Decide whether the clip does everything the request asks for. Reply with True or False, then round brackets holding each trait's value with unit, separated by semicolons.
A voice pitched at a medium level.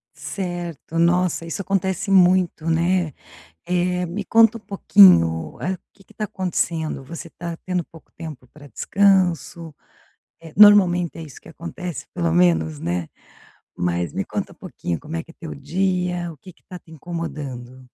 True (170 Hz)